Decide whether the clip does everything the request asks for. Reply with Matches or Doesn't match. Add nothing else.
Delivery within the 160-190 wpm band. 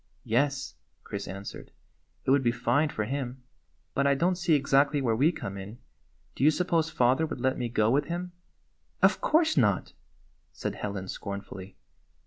Matches